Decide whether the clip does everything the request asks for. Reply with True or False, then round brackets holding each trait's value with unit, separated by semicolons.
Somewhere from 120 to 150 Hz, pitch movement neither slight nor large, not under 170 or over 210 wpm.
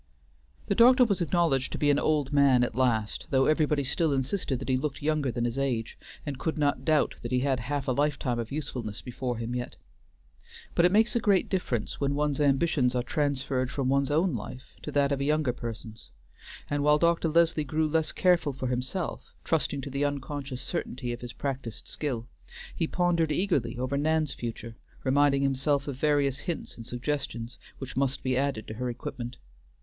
True (140 Hz; 3.2 semitones; 195 wpm)